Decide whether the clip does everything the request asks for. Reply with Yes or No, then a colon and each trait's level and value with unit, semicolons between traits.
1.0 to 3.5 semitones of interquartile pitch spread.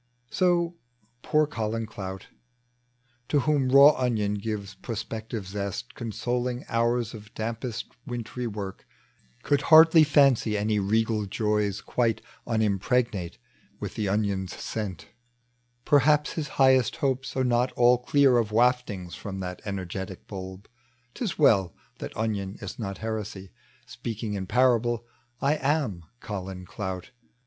No: average, 4.0 semitones